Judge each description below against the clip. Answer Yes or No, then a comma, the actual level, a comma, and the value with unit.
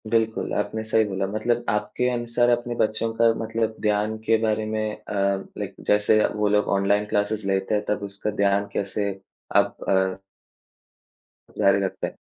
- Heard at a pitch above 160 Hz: No, low, 105 Hz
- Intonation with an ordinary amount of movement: No, narrow, 1.7 semitones